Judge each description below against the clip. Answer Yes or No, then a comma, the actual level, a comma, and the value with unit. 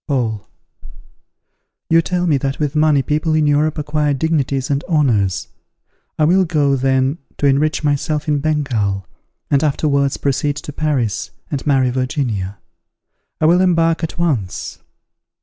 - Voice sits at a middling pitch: Yes, medium, 145 Hz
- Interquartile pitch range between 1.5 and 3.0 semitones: Yes, average, 2.7 semitones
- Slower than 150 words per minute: Yes, average, 140 wpm